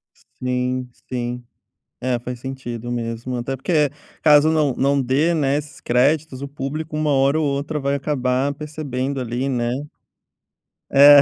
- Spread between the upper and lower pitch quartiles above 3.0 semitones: No, average, 2.7 semitones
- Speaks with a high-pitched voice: No, low, 135 Hz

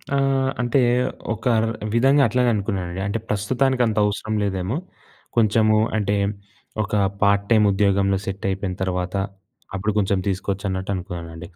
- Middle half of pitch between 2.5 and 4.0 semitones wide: Yes, average, 2.9 semitones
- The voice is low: Yes, low, 100 Hz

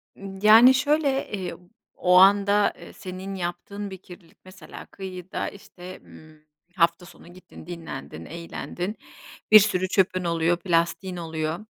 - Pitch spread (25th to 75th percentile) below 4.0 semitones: Yes, average, 2.8 semitones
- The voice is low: No, medium, 185 Hz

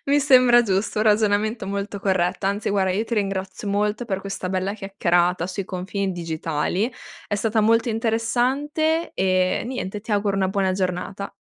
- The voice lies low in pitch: No, high, 200 Hz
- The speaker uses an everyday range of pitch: Yes, average, 3.0 semitones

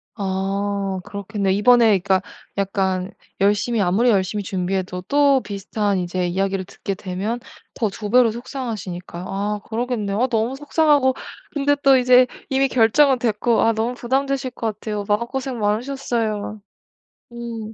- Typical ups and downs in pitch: Yes, average, 4.1 semitones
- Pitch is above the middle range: Yes, high, 220 Hz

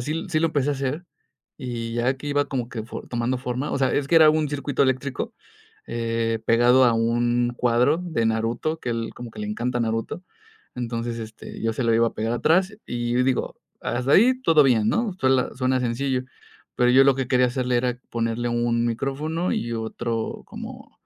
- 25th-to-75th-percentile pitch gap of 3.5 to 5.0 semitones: No, average, 3.0 semitones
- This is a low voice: Yes, low, 125 Hz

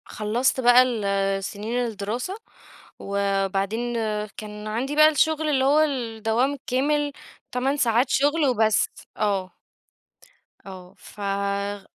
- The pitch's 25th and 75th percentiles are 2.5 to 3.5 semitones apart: No, average, 4.8 semitones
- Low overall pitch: No, high, 235 Hz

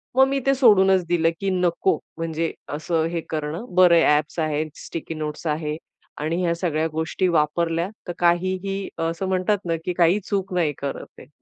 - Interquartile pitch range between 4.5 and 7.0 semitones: No, average, 2.8 semitones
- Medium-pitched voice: Yes, medium, 170 Hz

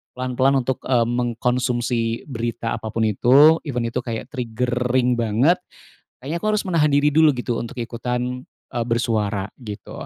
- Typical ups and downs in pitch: No, narrow, 2.1 semitones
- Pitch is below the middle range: Yes, low, 125 Hz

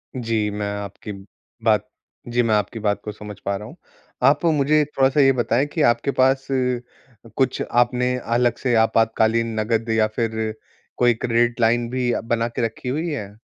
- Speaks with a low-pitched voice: Yes, low, 115 Hz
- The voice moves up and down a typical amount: No, narrow, 2.3 semitones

